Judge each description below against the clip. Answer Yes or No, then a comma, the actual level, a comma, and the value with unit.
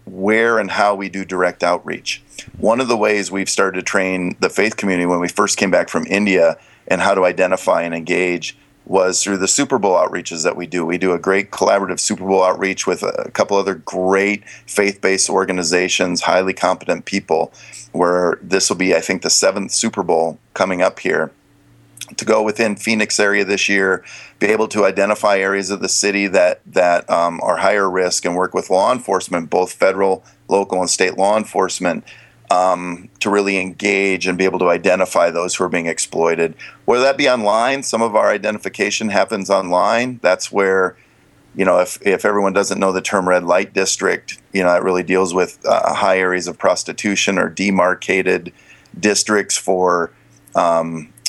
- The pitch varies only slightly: Yes, narrow, 2.1 semitones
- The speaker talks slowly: No, average, 185 wpm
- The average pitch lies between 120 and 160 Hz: No, very low, 95 Hz